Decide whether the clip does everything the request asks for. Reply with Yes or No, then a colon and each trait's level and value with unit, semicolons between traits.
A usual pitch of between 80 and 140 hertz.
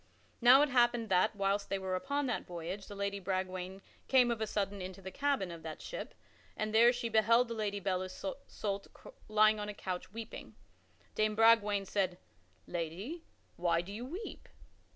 No: high, 205 Hz